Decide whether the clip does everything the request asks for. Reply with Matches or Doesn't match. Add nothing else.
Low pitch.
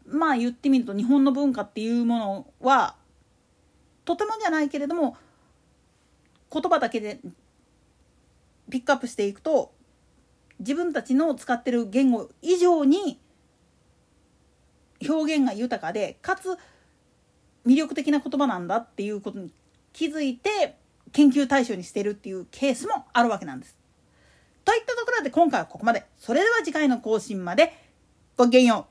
Doesn't match